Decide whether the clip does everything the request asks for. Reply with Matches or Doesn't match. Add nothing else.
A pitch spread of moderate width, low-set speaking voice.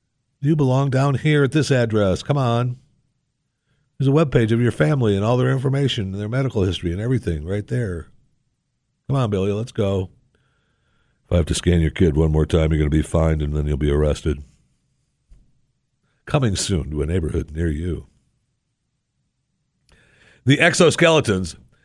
Doesn't match